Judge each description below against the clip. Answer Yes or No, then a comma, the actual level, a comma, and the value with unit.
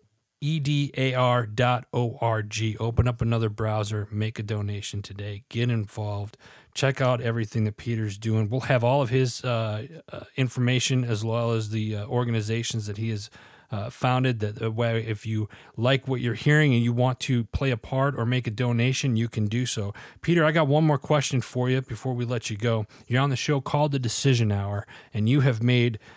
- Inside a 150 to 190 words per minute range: No, fast, 205 wpm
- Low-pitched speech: Yes, low, 120 Hz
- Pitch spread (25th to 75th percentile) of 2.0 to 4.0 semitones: Yes, average, 2.9 semitones